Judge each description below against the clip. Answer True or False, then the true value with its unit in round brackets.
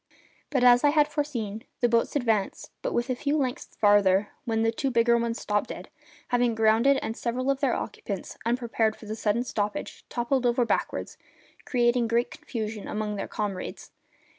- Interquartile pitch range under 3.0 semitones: True (2.5 semitones)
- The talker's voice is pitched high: True (235 Hz)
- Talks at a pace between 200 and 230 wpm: False (170 wpm)